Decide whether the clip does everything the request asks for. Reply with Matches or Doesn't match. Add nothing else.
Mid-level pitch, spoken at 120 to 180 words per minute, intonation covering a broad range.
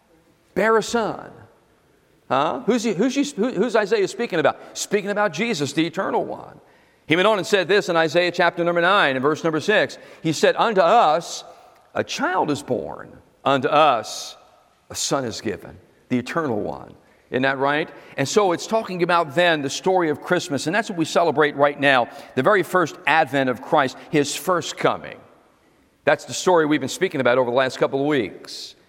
Doesn't match